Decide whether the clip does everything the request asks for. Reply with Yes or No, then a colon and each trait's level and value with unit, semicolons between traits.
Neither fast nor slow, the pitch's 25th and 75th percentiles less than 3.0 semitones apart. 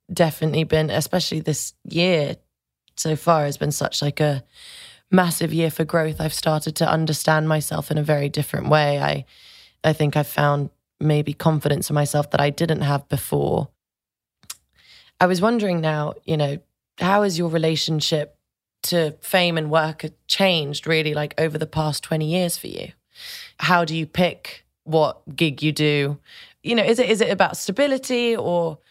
Yes: average, 170 wpm; narrow, 2.6 semitones